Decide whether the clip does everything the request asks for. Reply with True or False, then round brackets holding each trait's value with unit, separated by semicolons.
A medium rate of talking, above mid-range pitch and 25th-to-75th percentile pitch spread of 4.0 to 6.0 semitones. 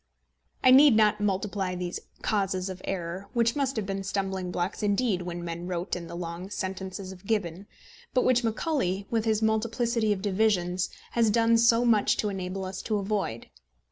False (175 wpm; 200 Hz; 3.2 semitones)